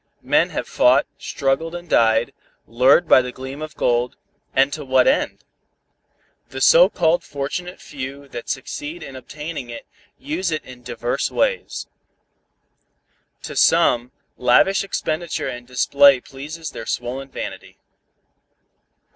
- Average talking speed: No, slow, 130 wpm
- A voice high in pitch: No, medium, 140 Hz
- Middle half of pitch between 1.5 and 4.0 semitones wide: No, average, 4.6 semitones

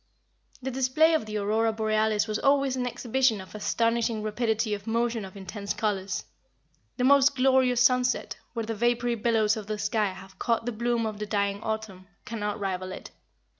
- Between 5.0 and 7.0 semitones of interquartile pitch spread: No, narrow, 2.6 semitones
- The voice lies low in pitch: No, high, 220 Hz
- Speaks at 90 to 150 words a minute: No, average, 175 wpm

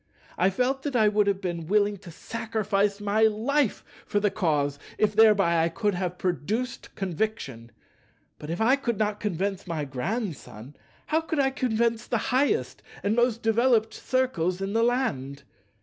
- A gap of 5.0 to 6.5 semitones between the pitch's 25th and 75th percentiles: No, average, 4.6 semitones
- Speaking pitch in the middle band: No, high, 210 Hz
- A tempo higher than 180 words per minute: No, average, 165 wpm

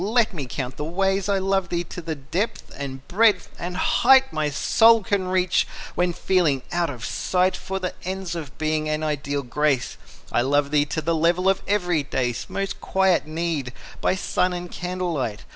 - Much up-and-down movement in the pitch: No, average, 4.4 semitones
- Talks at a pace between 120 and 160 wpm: No, average, 180 wpm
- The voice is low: No, medium, 175 Hz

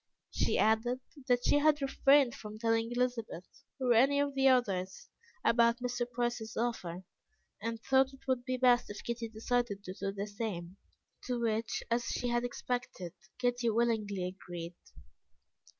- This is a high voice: Yes, high, 235 Hz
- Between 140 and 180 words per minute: Yes, average, 150 wpm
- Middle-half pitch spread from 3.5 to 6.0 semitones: No, average, 2.7 semitones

